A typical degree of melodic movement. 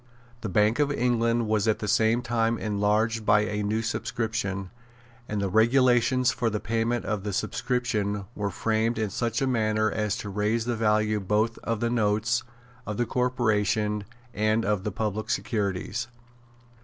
No: narrow, 1.9 semitones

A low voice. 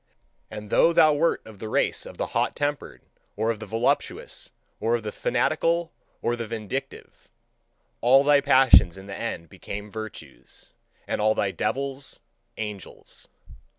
Yes: low, 115 Hz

